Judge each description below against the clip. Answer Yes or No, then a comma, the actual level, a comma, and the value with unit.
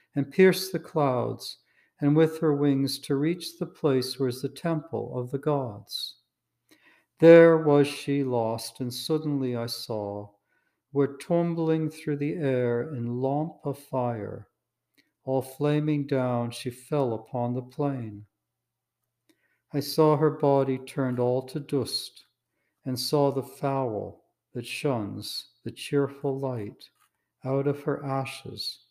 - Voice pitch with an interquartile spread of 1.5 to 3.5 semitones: Yes, average, 3.1 semitones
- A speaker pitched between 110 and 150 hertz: Yes, low, 135 Hz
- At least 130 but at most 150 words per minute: Yes, slow, 135 wpm